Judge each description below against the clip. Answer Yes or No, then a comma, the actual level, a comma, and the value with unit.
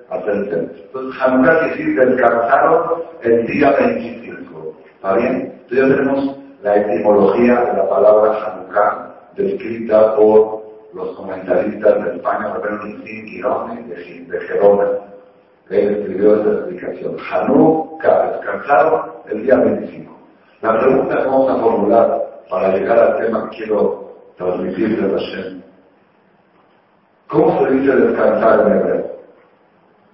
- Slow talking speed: Yes, slow, 120 wpm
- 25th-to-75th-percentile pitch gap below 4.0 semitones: No, average, 4.6 semitones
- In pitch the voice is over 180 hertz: No, low, 120 Hz